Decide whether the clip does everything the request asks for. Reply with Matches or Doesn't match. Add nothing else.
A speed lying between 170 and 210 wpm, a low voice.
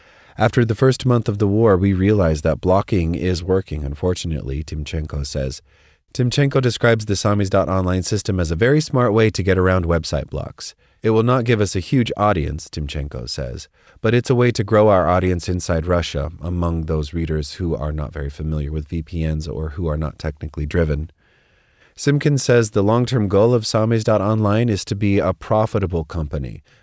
Matches